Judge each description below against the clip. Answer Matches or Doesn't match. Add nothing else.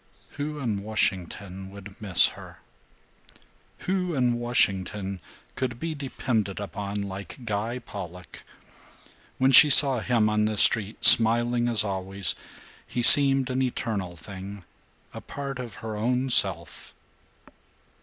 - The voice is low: Matches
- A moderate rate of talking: Doesn't match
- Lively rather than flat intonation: Doesn't match